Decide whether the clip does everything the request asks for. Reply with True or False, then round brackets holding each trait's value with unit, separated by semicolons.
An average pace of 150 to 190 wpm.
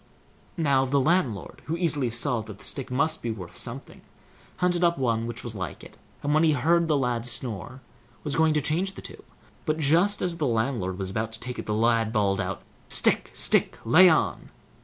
False (205 wpm)